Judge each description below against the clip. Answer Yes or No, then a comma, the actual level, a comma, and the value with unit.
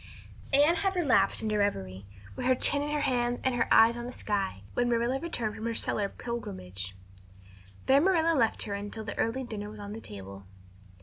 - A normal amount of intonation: Yes, average, 4.5 semitones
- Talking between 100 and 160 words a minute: No, average, 200 wpm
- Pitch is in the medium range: No, high, 230 Hz